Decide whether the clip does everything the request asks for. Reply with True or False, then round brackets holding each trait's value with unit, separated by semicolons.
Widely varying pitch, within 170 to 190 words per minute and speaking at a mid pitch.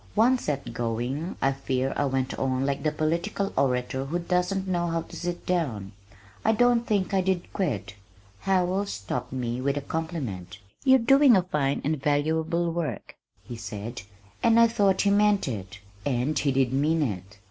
True (6.4 semitones; 175 wpm; 155 Hz)